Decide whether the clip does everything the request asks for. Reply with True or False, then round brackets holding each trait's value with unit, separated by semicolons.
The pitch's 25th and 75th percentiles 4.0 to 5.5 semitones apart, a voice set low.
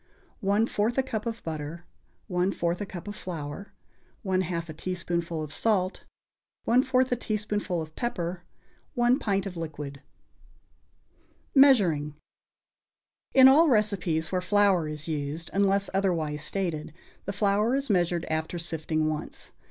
False (4.7 semitones; 180 Hz)